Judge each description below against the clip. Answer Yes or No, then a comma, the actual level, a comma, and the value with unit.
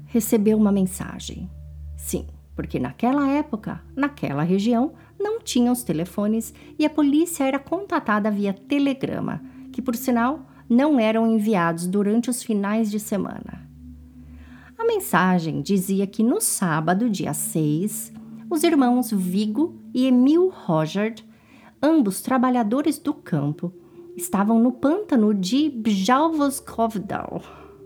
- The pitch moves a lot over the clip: Yes, wide, 6.4 semitones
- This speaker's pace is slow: Yes, slow, 115 wpm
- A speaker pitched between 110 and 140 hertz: No, high, 220 Hz